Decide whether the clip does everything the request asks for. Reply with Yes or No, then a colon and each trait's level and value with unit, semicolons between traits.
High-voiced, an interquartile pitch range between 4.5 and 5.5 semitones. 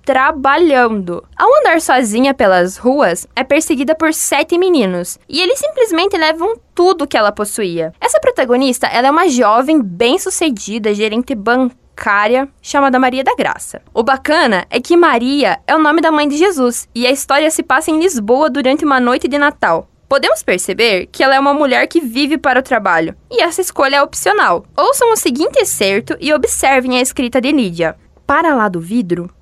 Yes: very high, 275 Hz; average, 4.8 semitones